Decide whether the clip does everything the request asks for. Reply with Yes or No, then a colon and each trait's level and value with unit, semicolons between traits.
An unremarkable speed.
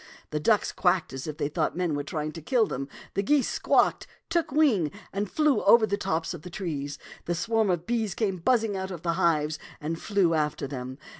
No: fast, 225 wpm